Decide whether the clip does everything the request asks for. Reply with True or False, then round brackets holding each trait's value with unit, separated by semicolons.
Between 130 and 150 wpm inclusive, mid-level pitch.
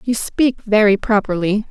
False (140 wpm; 210 Hz)